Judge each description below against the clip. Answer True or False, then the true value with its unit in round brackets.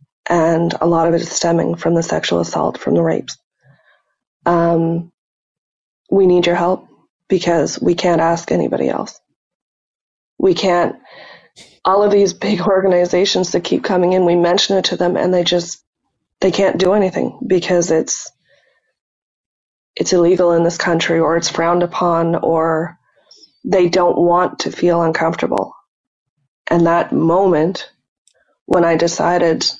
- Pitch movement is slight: True (1.6 semitones)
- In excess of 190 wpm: False (145 wpm)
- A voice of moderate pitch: True (175 Hz)